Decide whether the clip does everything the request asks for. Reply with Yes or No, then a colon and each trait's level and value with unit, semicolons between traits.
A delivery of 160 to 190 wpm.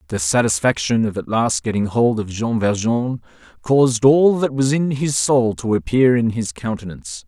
Yes: average, 180 wpm